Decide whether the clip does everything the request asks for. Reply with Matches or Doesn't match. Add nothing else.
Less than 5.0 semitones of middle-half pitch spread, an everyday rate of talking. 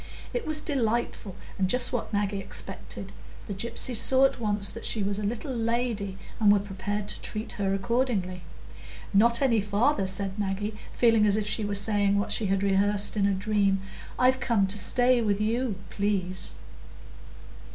Matches